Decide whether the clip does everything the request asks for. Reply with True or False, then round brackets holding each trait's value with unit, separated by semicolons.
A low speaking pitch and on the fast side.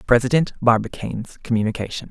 False (120 Hz; 85 wpm)